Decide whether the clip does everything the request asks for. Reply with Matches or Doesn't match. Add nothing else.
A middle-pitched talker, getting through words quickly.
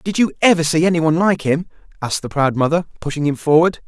Matches